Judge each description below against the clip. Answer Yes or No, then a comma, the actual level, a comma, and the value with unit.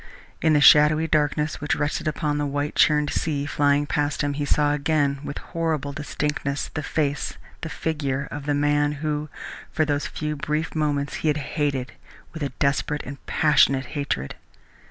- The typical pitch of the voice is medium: Yes, medium, 145 Hz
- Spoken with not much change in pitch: Yes, narrow, 1.1 semitones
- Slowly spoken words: No, average, 170 wpm